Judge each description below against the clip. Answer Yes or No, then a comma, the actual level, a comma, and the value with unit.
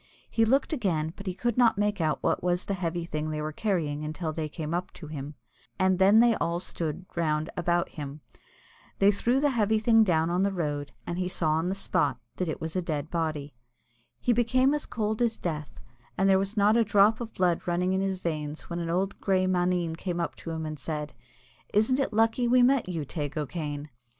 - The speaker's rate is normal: No, fast, 225 wpm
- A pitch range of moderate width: Yes, average, 4.9 semitones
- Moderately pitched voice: Yes, medium, 180 Hz